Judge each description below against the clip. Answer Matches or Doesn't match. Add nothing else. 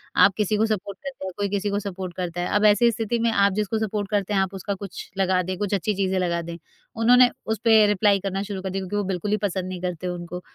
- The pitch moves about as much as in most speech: Doesn't match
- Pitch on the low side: Doesn't match